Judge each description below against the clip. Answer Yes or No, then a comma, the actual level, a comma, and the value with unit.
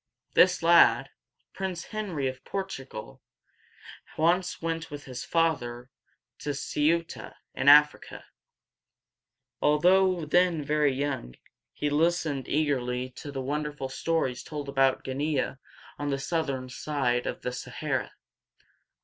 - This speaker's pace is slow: Yes, slow, 115 wpm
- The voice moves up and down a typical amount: Yes, average, 3.7 semitones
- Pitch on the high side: No, medium, 145 Hz